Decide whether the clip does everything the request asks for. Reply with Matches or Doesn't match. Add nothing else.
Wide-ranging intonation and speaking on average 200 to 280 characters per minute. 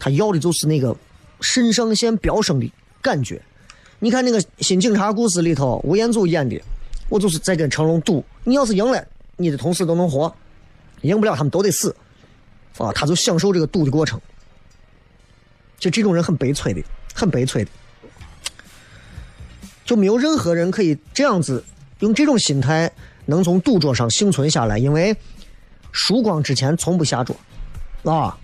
Matches